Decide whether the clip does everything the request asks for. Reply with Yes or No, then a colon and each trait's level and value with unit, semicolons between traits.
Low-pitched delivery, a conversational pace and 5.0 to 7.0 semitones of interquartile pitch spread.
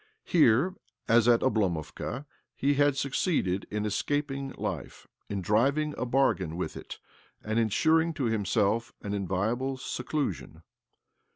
No: low, 120 Hz; slow, 120 wpm; average, 5.3 semitones